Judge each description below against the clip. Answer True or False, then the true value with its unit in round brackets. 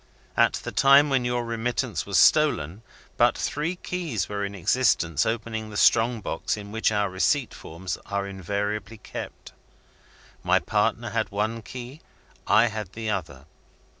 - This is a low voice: True (110 Hz)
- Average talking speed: True (150 wpm)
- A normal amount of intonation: True (3.4 semitones)